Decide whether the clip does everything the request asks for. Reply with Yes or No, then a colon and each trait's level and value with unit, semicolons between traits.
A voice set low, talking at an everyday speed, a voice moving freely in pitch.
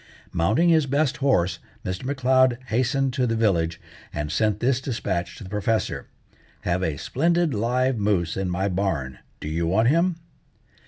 Yes: low, 110 Hz; average, 160 wpm; wide, 6.5 semitones